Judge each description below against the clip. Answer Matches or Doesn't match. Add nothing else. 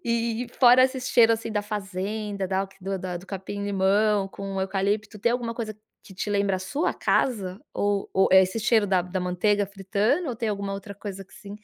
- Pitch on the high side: Matches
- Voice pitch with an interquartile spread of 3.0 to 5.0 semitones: Doesn't match